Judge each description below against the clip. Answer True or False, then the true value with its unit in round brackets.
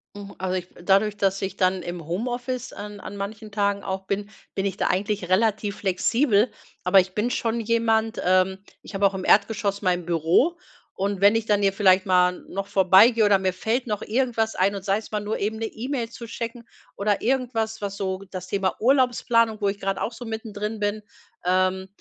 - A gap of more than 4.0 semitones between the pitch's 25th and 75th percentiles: False (2.7 semitones)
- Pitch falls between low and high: False (205 Hz)